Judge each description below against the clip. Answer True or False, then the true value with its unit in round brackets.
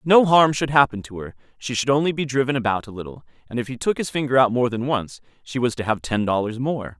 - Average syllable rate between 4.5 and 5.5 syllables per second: False (6.1 syllables/s)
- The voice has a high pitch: False (125 Hz)